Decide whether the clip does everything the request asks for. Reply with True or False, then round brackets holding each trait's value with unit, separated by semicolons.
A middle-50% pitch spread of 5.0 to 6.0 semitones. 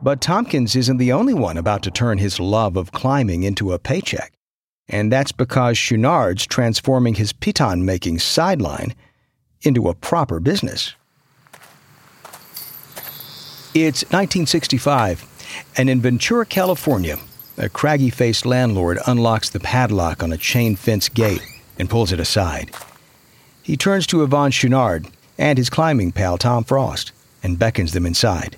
True (5.5 semitones)